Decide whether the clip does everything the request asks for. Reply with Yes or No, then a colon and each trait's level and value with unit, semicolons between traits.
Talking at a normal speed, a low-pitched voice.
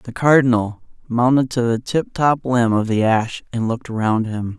Yes: average, 195 wpm; low, 120 Hz